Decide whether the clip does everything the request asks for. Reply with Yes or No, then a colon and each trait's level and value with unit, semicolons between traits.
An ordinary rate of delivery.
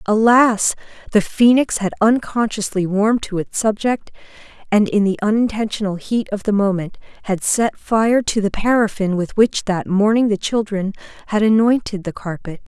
Yes: average, 155 wpm